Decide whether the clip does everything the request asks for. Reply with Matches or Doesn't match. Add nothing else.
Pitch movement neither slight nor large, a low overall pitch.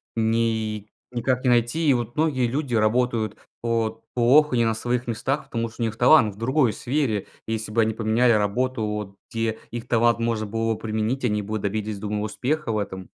Doesn't match